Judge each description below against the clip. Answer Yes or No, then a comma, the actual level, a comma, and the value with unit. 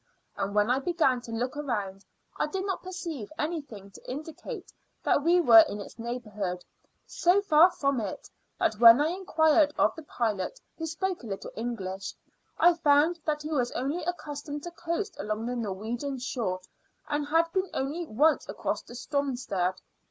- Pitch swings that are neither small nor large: No, wide, 6.3 semitones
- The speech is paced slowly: No, average, 170 wpm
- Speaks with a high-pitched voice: Yes, very high, 280 Hz